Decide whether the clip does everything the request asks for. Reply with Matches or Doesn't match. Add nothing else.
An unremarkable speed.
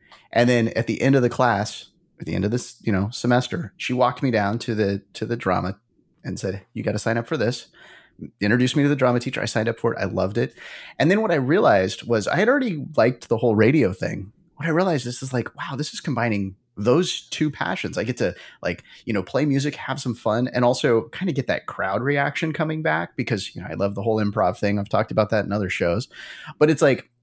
Doesn't match